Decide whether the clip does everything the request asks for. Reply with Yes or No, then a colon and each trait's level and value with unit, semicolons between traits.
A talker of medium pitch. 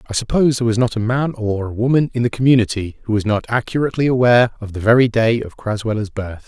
No: low, 115 Hz